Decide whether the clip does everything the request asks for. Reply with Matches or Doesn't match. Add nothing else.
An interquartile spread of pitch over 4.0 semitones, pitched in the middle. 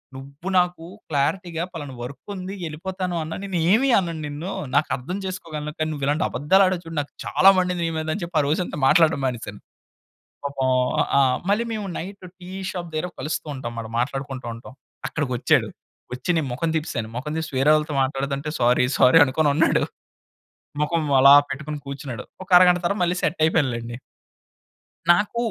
Matches